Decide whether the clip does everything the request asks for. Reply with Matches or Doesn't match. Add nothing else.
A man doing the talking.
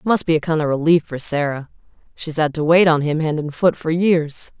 Doesn't match